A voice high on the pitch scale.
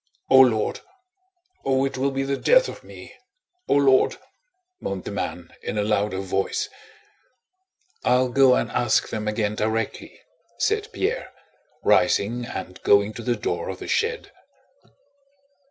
No: low, 120 Hz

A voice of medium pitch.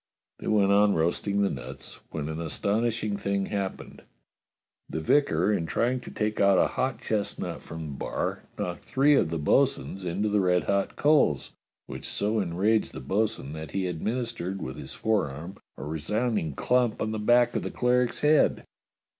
No: low, 100 Hz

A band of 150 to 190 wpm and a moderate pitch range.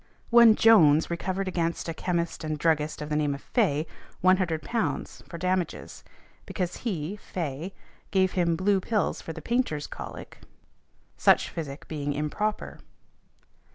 No: slow, 135 wpm; average, 4.0 semitones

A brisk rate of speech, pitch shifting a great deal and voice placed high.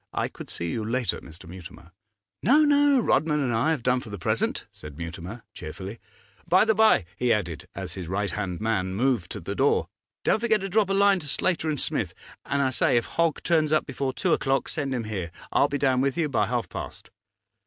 No: fast, 220 wpm; wide, 8.8 semitones; low, 130 Hz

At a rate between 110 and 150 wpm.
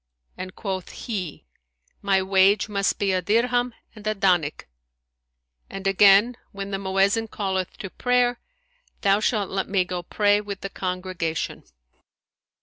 Yes: average, 140 wpm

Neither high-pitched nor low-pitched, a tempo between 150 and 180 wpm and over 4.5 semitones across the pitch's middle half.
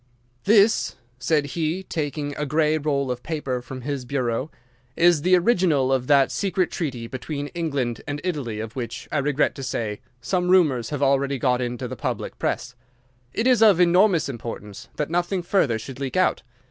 Yes: medium, 145 Hz; average, 175 wpm; average, 5.3 semitones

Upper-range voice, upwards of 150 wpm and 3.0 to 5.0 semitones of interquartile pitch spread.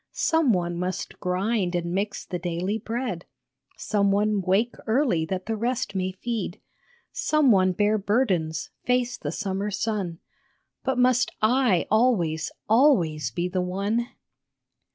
No: high, 200 Hz; slow, 135 wpm; average, 4.7 semitones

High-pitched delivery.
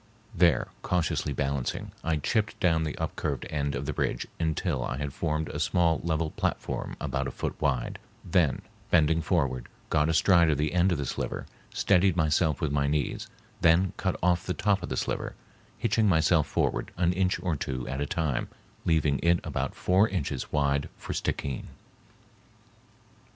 No: very low, 80 Hz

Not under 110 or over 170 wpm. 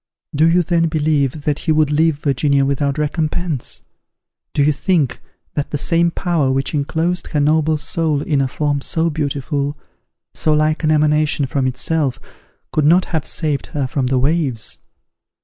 Yes: average, 165 wpm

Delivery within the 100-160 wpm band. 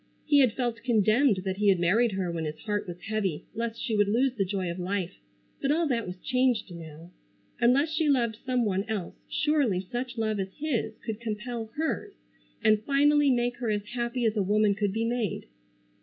No: average, 200 wpm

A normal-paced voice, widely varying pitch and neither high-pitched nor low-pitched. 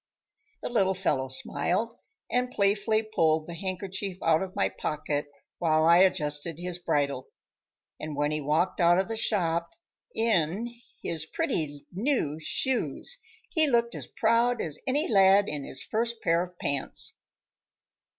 Yes: average, 145 wpm; wide, 6.0 semitones; medium, 180 Hz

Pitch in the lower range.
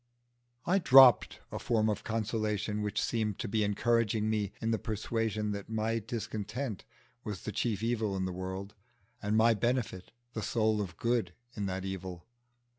Yes: low, 110 Hz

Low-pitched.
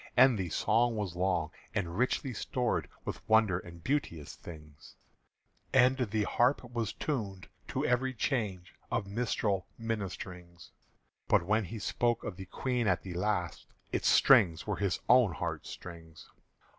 Yes: low, 105 Hz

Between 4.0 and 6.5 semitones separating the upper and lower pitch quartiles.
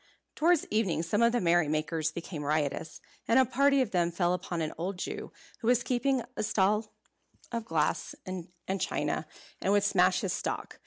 Yes: wide, 5.5 semitones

